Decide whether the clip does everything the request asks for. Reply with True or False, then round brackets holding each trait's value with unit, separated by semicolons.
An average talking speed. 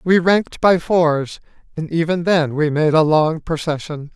True (175 wpm)